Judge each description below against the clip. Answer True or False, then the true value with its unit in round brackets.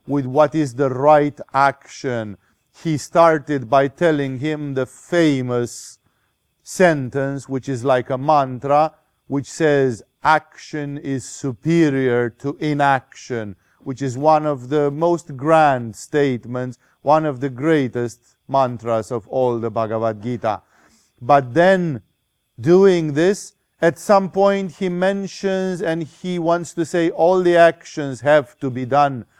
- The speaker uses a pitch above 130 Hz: True (140 Hz)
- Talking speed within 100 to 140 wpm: True (135 wpm)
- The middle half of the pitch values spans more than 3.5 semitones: True (4.0 semitones)